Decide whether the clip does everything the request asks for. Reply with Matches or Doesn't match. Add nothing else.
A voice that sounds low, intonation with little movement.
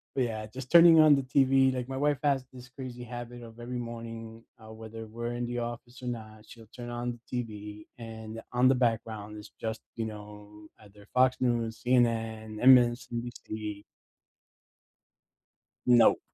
Matches